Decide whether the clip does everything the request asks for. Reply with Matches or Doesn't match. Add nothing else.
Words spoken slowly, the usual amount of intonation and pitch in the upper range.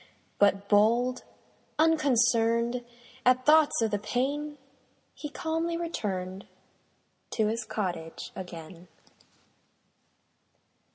Doesn't match